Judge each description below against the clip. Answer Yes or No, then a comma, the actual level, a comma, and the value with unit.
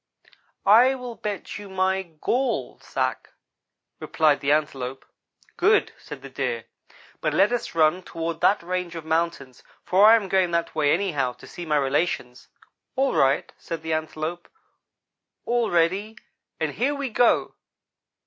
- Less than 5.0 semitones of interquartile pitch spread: No, wide, 5.4 semitones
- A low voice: No, medium, 175 Hz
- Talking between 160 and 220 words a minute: No, average, 150 wpm